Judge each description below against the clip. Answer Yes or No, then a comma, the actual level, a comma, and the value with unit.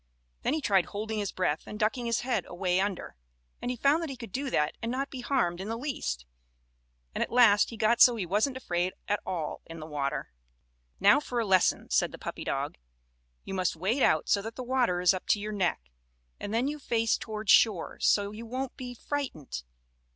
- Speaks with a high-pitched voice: Yes, high, 215 Hz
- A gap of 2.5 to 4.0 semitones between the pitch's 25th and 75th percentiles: No, average, 5.3 semitones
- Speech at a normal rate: No, fast, 215 wpm